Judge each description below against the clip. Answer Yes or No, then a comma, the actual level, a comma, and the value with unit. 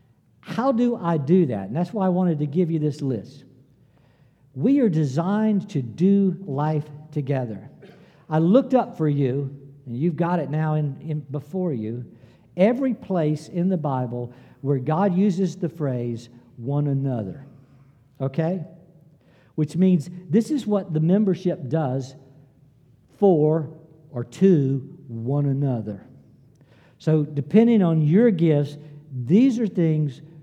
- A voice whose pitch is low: No, medium, 155 Hz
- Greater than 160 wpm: No, average, 140 wpm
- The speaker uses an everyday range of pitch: Yes, average, 4.8 semitones